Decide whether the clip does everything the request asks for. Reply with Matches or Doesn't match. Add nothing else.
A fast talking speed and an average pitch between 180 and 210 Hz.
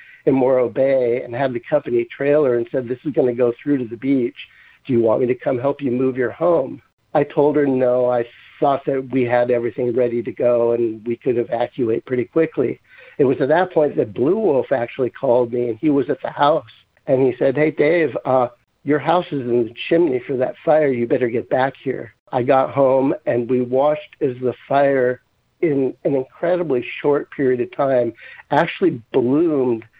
Doesn't match